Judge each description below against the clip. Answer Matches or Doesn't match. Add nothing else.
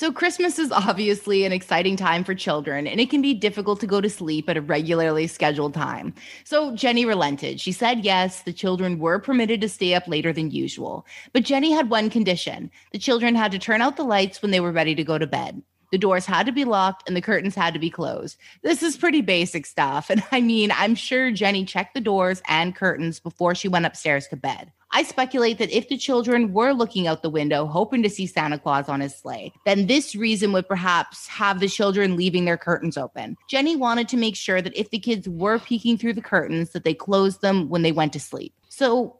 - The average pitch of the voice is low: Doesn't match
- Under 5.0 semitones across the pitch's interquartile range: Doesn't match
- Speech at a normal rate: Doesn't match